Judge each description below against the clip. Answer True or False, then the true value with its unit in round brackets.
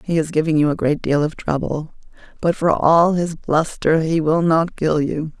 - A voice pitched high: False (160 Hz)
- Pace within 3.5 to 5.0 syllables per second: True (4.6 syllables/s)